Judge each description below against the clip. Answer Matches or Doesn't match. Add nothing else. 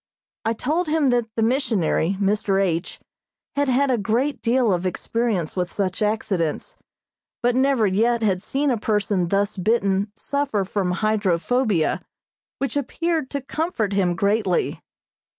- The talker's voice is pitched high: Matches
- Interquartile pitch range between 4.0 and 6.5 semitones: Matches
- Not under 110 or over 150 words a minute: Matches